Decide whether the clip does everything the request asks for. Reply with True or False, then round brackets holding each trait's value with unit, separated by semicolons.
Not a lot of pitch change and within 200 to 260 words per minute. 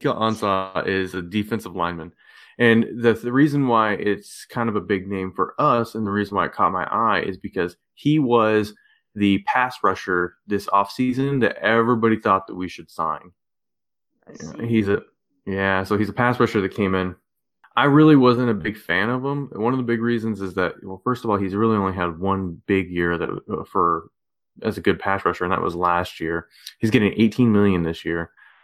False (3.6 semitones; 205 wpm)